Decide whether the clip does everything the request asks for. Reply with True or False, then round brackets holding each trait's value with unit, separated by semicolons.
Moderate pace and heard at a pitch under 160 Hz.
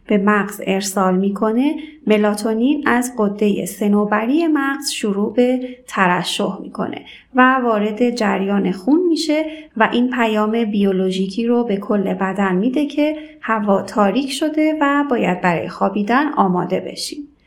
False (125 wpm; 220 Hz)